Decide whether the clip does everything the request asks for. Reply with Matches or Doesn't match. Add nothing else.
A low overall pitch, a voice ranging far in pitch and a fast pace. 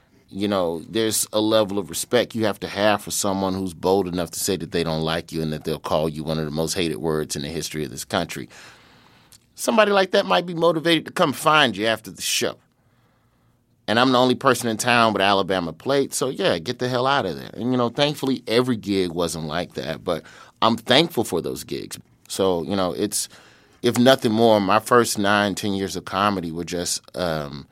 Matches